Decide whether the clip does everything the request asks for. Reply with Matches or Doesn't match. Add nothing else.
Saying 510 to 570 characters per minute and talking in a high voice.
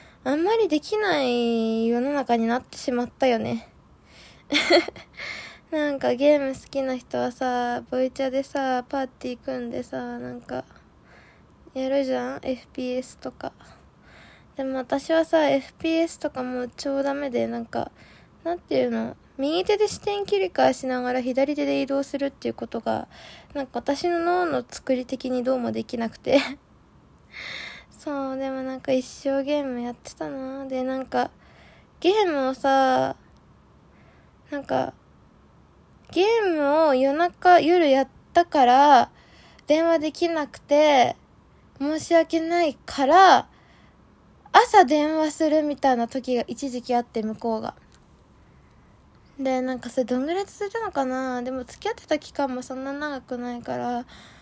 Doesn't match